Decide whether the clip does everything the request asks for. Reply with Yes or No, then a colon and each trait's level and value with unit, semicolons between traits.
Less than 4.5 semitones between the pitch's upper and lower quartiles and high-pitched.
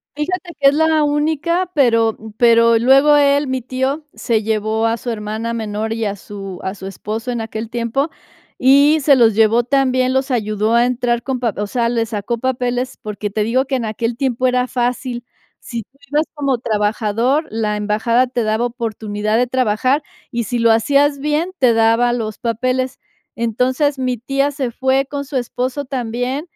Yes: average, 3.3 semitones; high, 245 Hz